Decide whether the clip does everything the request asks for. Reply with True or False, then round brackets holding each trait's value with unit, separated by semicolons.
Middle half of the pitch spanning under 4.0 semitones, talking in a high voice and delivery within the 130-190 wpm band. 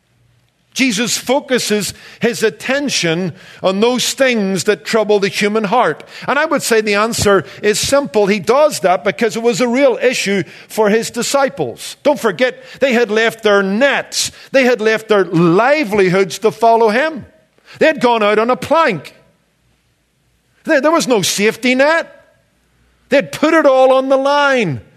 False (4.6 semitones; 230 Hz; 160 wpm)